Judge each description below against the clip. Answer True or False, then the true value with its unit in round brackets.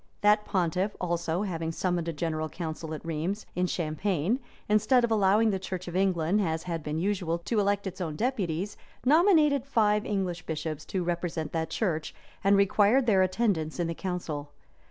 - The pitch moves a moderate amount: True (4.2 semitones)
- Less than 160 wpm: False (175 wpm)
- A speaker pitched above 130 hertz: True (185 Hz)